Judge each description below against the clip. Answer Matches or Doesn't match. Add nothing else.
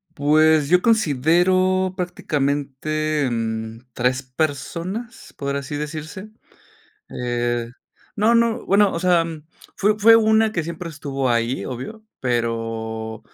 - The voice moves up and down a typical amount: Doesn't match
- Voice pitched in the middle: Matches